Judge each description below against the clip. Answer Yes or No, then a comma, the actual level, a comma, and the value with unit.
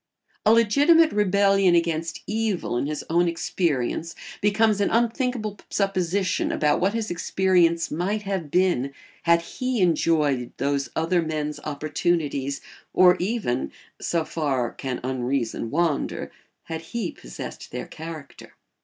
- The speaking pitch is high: No, medium, 170 Hz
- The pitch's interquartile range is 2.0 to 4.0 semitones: No, average, 5.1 semitones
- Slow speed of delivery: Yes, slow, 125 wpm